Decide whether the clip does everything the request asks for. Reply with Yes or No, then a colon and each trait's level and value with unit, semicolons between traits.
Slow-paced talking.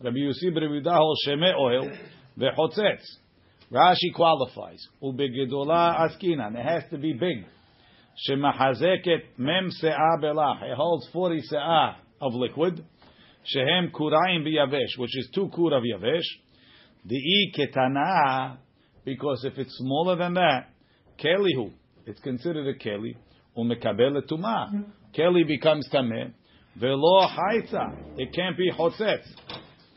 Yes: slow, 115 wpm